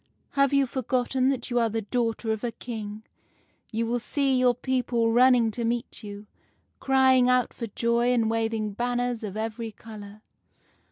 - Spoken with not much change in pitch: Yes, narrow, 2.1 semitones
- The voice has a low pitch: No, high, 235 Hz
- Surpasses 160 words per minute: Yes, average, 170 wpm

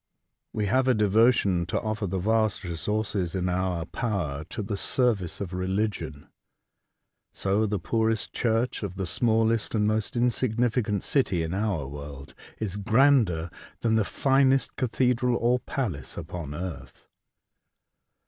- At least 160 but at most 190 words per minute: No, average, 140 wpm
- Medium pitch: No, low, 105 Hz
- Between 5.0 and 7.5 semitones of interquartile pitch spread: No, average, 4.3 semitones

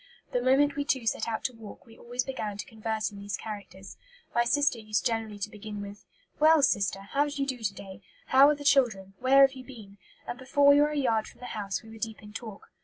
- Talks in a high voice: Yes, high, 225 Hz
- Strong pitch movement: No, average, 4.5 semitones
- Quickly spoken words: Yes, fast, 250 wpm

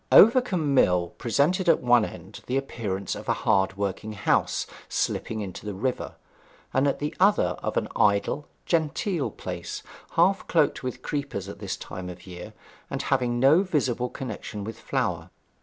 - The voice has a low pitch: Yes, low, 125 Hz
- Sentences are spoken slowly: No, average, 165 wpm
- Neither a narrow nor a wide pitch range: No, wide, 6.9 semitones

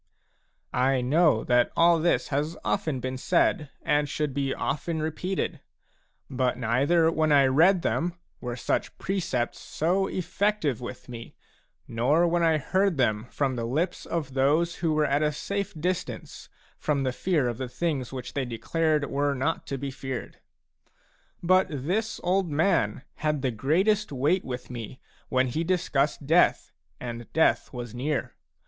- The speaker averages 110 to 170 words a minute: Yes, average, 155 wpm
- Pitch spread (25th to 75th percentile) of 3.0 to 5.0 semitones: Yes, average, 4.7 semitones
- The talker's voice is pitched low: No, medium, 145 Hz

